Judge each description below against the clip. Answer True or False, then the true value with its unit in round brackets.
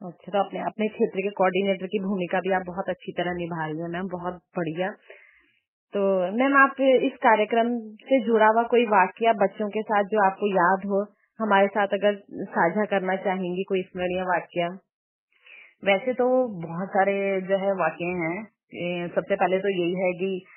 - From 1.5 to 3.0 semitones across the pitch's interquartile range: True (2.7 semitones)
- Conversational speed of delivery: True (160 wpm)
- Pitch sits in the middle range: False (195 Hz)